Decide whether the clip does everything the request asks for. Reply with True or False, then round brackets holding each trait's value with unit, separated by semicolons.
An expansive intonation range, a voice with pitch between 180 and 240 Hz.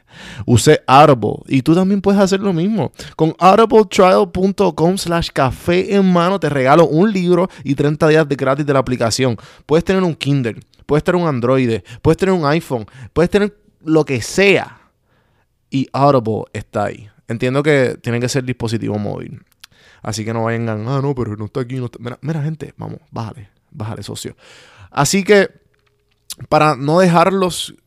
False (6.1 semitones; 140 Hz)